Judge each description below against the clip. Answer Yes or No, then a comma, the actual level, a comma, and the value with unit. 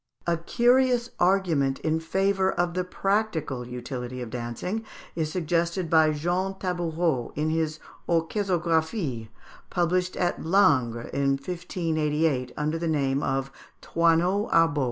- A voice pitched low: No, medium, 165 Hz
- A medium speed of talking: No, slow, 120 wpm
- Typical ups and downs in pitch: Yes, average, 4.0 semitones